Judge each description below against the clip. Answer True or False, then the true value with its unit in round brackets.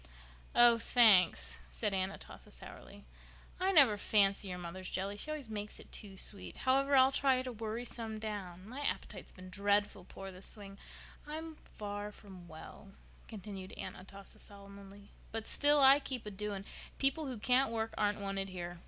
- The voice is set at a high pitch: True (205 Hz)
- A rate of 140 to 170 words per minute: True (165 wpm)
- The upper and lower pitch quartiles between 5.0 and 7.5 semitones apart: False (4.0 semitones)